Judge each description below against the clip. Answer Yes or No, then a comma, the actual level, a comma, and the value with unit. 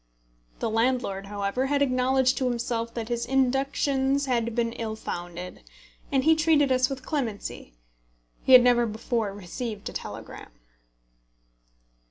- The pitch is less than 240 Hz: No, high, 245 Hz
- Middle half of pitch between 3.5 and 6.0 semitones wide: No, average, 3.1 semitones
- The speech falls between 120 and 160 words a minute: Yes, slow, 135 wpm